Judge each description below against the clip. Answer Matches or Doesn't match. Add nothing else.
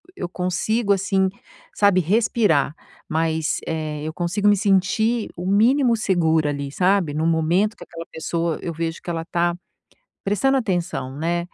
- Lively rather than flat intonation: Doesn't match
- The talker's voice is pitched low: Doesn't match